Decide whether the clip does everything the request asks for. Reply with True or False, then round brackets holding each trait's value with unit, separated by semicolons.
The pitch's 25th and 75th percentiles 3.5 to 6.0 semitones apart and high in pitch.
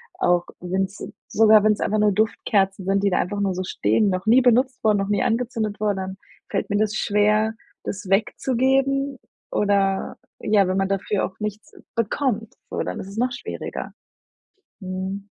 False (2.4 semitones; 205 Hz)